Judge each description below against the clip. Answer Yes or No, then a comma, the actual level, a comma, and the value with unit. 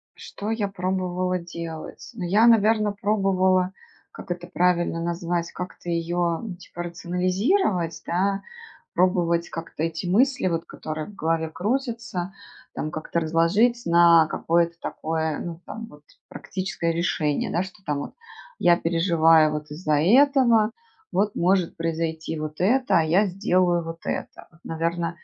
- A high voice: No, medium, 175 Hz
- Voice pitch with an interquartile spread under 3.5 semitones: Yes, average, 2.9 semitones